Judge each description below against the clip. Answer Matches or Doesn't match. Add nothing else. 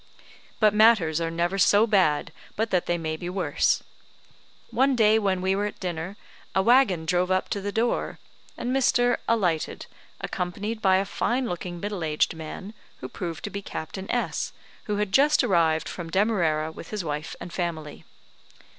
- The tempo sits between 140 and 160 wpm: Doesn't match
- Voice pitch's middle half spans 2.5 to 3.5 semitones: Doesn't match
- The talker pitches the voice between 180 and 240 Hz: Matches